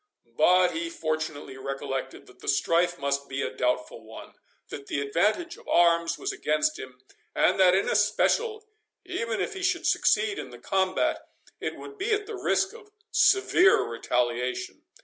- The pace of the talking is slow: No, average, 155 wpm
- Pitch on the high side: No, medium, 175 Hz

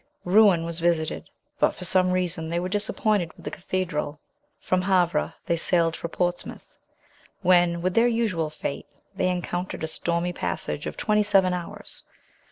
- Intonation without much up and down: Yes, narrow, 1.8 semitones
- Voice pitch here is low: No, medium, 180 Hz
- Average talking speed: Yes, average, 160 wpm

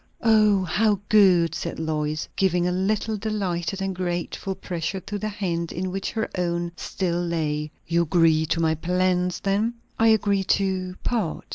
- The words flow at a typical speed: Yes, average, 160 wpm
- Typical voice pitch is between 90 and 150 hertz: No, medium, 185 Hz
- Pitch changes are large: No, average, 2.9 semitones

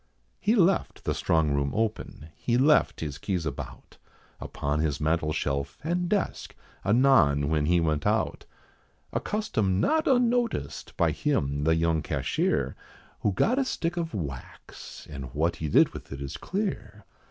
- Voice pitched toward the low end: Yes, very low, 85 Hz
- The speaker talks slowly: No, average, 155 wpm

